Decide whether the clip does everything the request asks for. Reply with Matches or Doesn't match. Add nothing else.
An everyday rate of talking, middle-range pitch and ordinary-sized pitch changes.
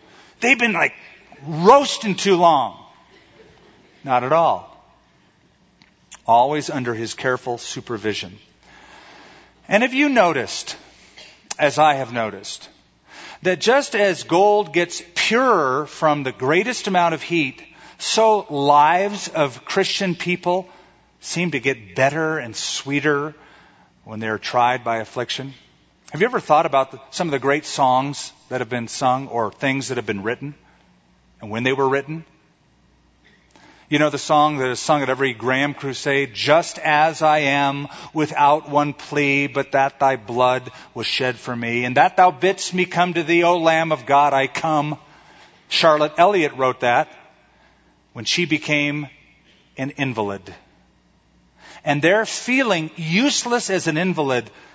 Matches